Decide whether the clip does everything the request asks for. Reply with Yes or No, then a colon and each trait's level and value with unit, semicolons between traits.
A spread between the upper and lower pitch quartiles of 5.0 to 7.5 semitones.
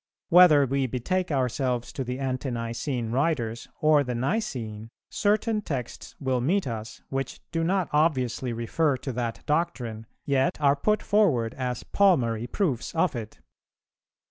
Yes: average, 5.3 semitones